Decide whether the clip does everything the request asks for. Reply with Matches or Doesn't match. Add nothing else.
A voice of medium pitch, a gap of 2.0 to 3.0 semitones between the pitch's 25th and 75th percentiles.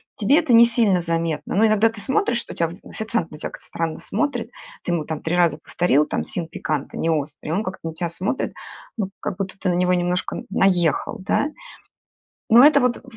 Doesn't match